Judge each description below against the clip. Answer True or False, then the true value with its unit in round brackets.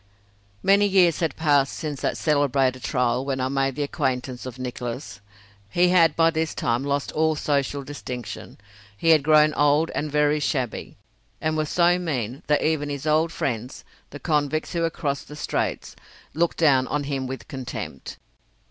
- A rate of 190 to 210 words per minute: False (170 wpm)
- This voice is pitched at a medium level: True (145 Hz)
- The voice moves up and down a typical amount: True (3.1 semitones)